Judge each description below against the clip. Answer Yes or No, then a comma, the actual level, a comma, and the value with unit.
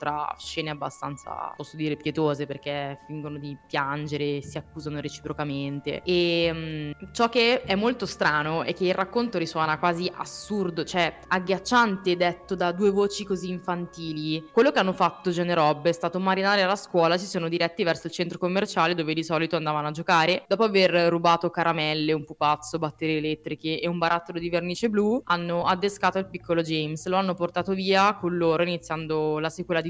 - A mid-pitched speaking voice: Yes, medium, 170 Hz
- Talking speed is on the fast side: Yes, fast, 175 wpm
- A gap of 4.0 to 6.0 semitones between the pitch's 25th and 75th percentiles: No, average, 2.9 semitones